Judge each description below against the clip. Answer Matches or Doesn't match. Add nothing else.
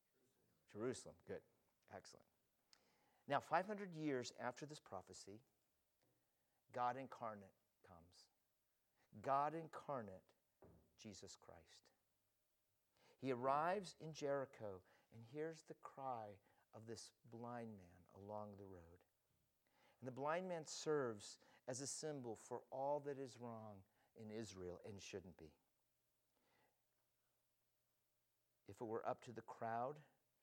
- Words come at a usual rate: Doesn't match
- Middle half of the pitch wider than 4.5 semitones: Matches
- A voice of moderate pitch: Doesn't match